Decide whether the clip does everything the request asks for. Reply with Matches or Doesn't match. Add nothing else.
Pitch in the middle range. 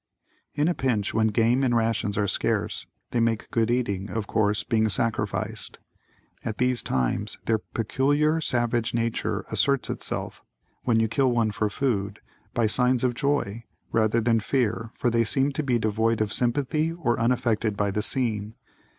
Doesn't match